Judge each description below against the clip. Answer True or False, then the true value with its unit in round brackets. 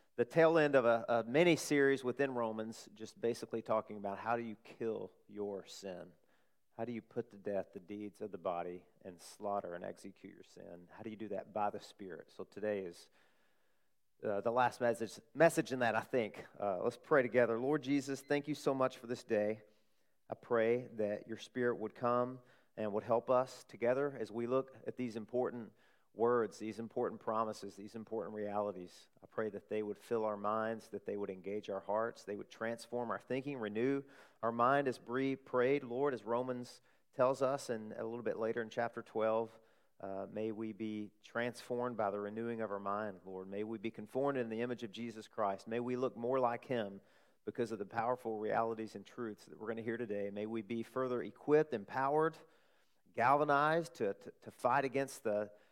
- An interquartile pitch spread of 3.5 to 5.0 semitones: False (2.8 semitones)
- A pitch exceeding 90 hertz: True (115 Hz)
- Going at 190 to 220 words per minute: True (200 wpm)